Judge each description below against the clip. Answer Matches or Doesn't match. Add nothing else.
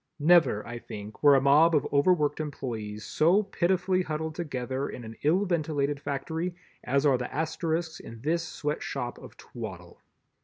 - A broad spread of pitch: Doesn't match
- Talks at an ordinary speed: Matches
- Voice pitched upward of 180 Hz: Doesn't match